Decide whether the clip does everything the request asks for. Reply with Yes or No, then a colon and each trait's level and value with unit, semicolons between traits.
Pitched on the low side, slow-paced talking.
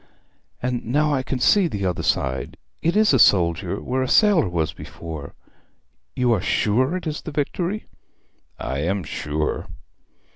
No: low, 120 Hz; average, 155 wpm